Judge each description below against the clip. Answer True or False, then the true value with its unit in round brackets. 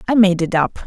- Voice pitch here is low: False (190 Hz)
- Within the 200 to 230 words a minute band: False (275 wpm)